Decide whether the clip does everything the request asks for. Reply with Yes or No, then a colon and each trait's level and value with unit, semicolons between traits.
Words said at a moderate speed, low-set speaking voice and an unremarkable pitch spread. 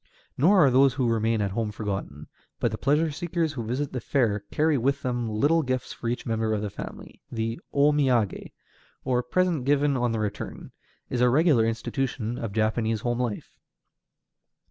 Yes: average, 190 wpm; low, 125 Hz; average, 4.0 semitones